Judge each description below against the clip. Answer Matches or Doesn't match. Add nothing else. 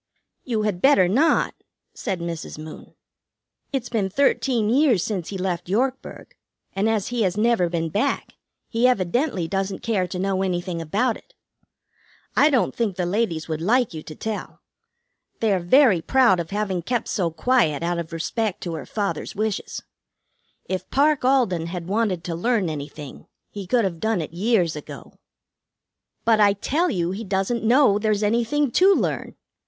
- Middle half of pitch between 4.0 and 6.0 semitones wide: Matches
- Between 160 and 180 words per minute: Matches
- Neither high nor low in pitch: Doesn't match